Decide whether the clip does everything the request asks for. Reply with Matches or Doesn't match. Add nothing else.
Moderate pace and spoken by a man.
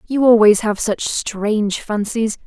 Doesn't match